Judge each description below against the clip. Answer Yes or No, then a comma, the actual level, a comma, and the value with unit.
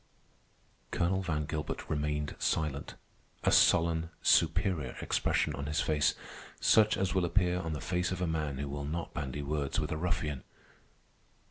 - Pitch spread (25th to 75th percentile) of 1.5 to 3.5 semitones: Yes, average, 3.2 semitones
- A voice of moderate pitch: No, very low, 80 Hz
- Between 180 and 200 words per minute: No, average, 155 wpm